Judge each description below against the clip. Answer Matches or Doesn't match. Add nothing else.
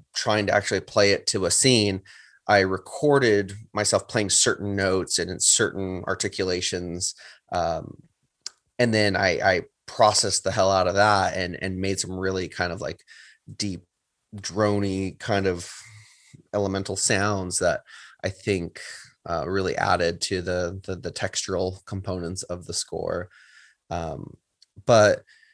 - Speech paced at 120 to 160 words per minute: Matches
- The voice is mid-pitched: Doesn't match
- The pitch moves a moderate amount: Doesn't match